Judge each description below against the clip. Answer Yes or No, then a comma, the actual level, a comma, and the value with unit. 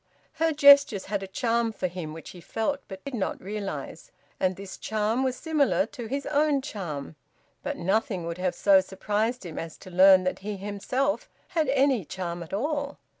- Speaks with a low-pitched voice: No, high, 210 Hz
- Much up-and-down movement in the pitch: Yes, wide, 6.7 semitones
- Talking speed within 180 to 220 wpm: Yes, average, 185 wpm